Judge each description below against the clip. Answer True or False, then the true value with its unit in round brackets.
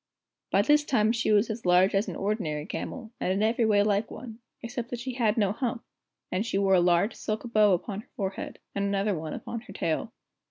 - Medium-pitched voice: False (210 Hz)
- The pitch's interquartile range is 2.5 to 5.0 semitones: True (2.9 semitones)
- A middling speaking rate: False (225 wpm)